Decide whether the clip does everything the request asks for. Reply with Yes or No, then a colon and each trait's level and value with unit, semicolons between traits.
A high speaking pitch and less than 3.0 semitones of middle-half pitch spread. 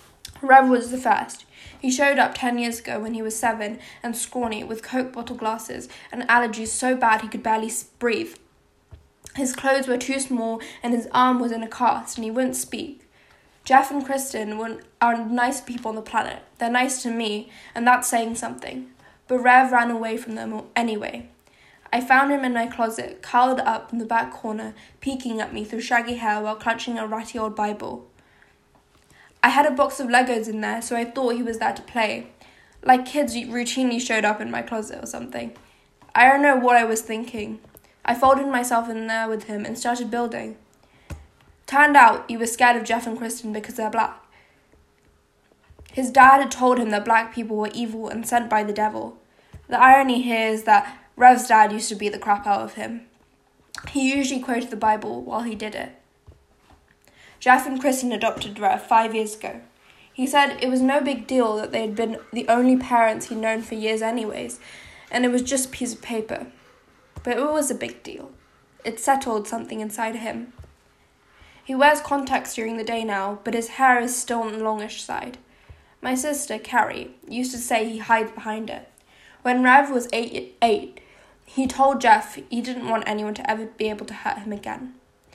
Yes: high, 235 Hz; narrow, 2.4 semitones